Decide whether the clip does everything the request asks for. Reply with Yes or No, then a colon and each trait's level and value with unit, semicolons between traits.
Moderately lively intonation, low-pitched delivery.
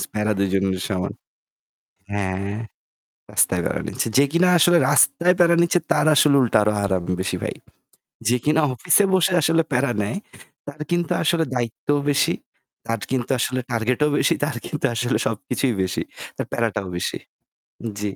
No: wide, 6.9 semitones; low, 125 Hz